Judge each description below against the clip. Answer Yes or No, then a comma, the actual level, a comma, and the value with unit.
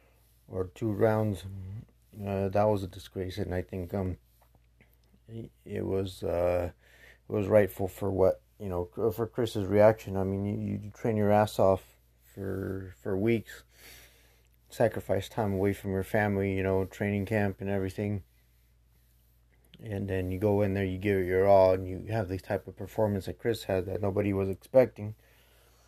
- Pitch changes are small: Yes, narrow, 2.2 semitones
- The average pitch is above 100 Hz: No, very low, 95 Hz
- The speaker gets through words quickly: No, average, 170 wpm